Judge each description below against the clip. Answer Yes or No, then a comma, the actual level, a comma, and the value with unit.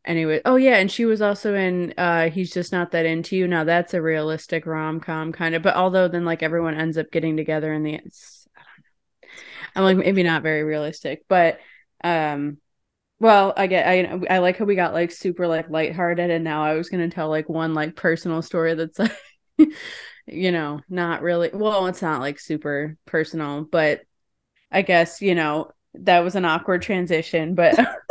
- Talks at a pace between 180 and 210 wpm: Yes, average, 200 wpm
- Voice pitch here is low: No, medium, 170 Hz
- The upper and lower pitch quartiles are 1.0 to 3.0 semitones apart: Yes, average, 2.7 semitones